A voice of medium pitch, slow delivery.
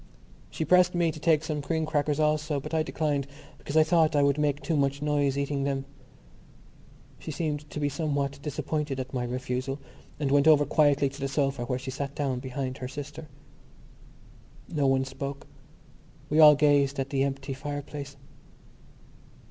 No: medium, 145 Hz; average, 170 wpm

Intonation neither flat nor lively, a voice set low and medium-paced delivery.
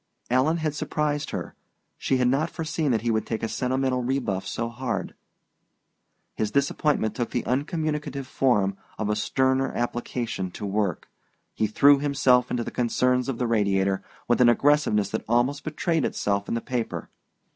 Yes: average, 4.1 semitones; low, 125 Hz; average, 165 wpm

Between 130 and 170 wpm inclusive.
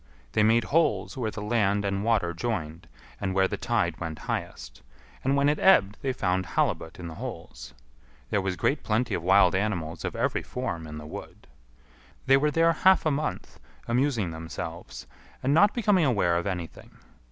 No: average, 180 wpm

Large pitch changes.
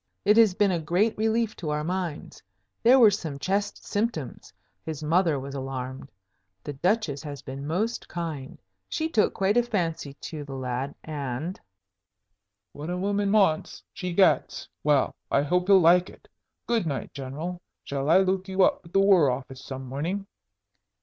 Yes: wide, 5.9 semitones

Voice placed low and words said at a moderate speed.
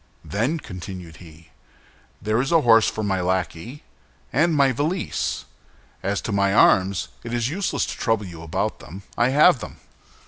Yes: low, 110 Hz; average, 165 wpm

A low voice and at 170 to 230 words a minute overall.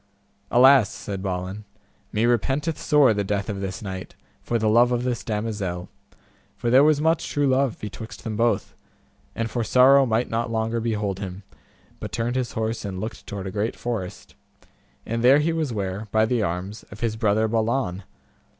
Yes: low, 110 Hz; average, 180 wpm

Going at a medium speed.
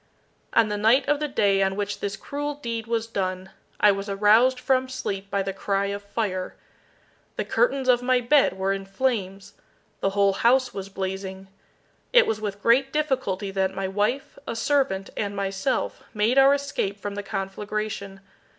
Yes: average, 175 wpm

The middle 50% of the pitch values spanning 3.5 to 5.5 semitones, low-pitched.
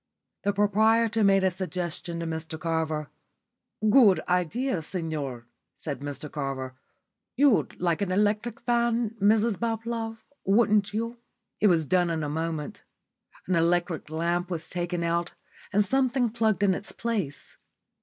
No: average, 5.2 semitones; medium, 185 Hz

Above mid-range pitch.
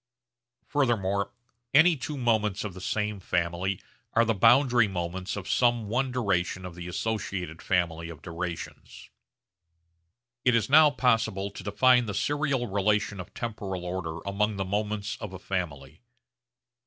No: low, 100 Hz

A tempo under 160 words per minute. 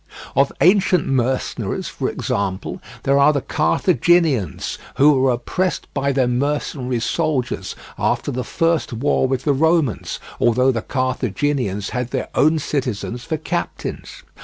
Yes: slow, 135 wpm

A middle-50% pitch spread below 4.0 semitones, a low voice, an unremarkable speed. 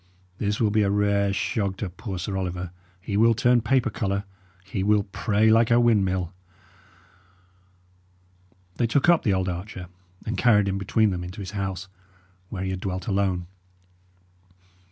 Yes: average, 2.7 semitones; low, 100 Hz; average, 160 wpm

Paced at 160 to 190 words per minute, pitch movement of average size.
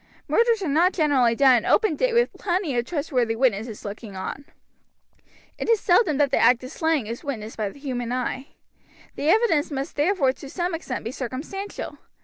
No: average, 180 wpm; wide, 6.2 semitones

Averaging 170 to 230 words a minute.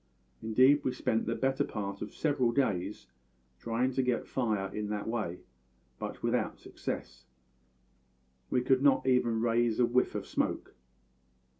No: average, 145 wpm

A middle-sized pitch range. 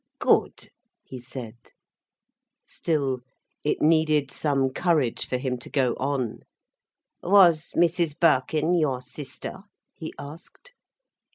Yes: average, 3.9 semitones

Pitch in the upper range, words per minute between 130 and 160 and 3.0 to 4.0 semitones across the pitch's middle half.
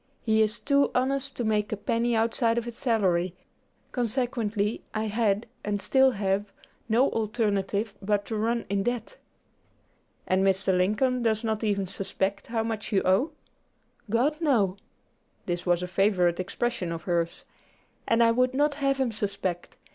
Yes: high, 220 Hz; average, 155 wpm; average, 3.4 semitones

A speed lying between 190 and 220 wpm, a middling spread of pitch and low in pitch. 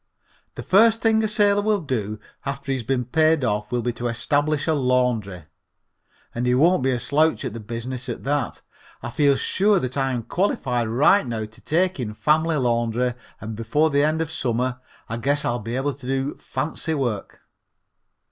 Yes: average, 195 wpm; average, 4.7 semitones; low, 130 Hz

